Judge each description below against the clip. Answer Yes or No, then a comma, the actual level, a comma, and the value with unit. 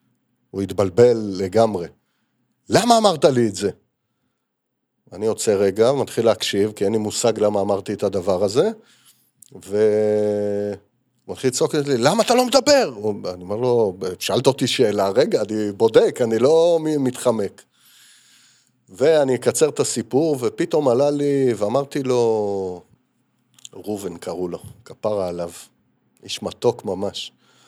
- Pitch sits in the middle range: No, low, 115 Hz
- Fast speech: No, average, 130 wpm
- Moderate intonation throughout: No, wide, 6.4 semitones